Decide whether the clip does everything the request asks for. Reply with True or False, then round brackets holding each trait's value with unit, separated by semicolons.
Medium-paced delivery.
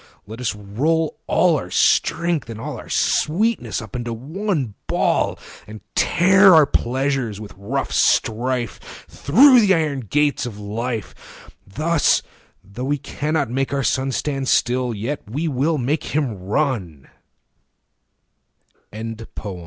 False (120 wpm)